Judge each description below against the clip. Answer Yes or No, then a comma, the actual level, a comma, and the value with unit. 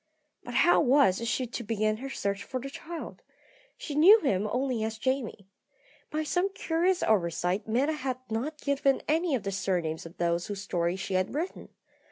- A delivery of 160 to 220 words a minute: Yes, average, 180 wpm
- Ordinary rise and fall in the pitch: No, wide, 6.6 semitones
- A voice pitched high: Yes, high, 240 Hz